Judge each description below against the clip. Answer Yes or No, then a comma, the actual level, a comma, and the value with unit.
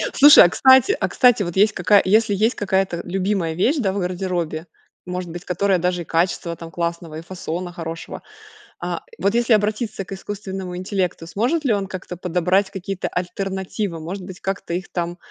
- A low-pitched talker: No, medium, 185 Hz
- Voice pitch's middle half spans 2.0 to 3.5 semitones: Yes, narrow, 2.6 semitones